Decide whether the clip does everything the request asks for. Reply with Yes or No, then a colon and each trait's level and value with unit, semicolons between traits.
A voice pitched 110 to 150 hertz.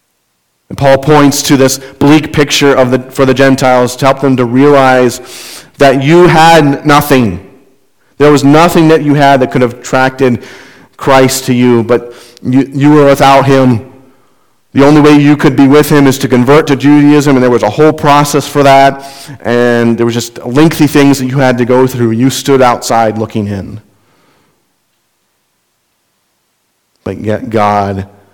Yes: low, 135 Hz